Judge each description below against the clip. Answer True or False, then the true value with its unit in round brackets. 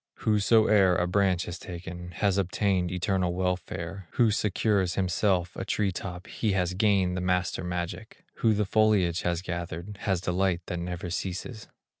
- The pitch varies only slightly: True (2.2 semitones)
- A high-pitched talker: False (90 Hz)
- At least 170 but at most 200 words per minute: False (155 wpm)